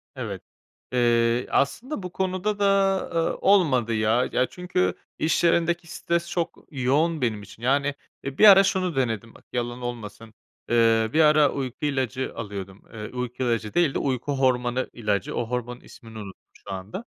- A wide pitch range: Yes, wide, 6.4 semitones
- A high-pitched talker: No, low, 130 Hz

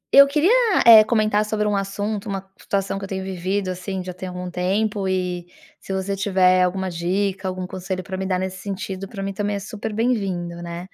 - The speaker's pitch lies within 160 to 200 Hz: Yes, high, 190 Hz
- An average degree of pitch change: No, narrow, 1.8 semitones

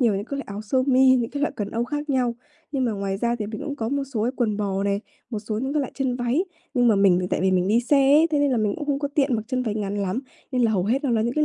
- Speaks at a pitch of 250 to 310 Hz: No, high, 240 Hz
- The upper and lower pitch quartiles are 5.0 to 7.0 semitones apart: No, average, 4.6 semitones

